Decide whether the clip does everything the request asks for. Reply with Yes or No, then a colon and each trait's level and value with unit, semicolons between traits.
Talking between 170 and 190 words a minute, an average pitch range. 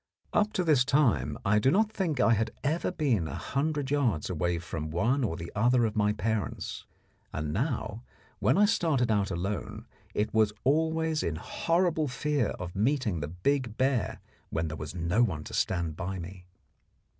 No: average, 175 wpm; wide, 8.4 semitones